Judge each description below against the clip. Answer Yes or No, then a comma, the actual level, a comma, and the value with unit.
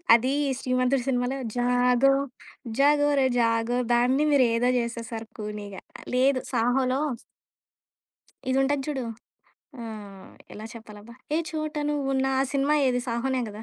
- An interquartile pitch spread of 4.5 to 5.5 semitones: No, average, 2.7 semitones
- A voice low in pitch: No, very high, 250 Hz